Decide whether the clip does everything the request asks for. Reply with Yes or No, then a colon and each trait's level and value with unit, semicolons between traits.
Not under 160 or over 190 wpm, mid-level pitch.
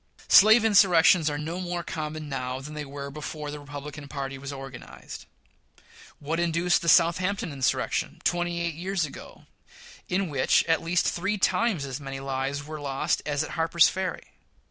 Yes: average, 165 wpm; medium, 155 Hz